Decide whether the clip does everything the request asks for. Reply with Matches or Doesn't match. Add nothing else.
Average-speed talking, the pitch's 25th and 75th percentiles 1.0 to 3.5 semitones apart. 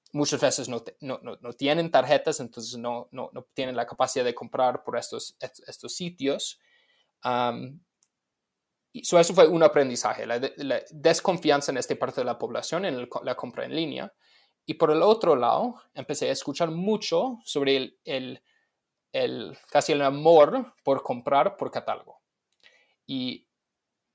Doesn't match